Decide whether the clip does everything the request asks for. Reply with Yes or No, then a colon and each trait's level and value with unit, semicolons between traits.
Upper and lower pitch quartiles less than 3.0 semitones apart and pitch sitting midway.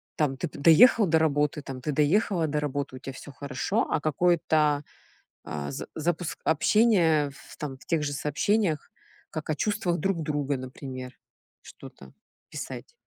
No: average, 3.4 semitones; medium, 150 Hz